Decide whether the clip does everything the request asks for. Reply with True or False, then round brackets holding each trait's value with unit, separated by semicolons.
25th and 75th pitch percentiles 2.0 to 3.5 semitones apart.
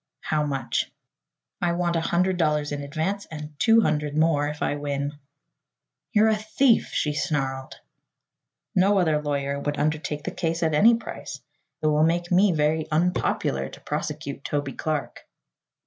True (3.1 semitones)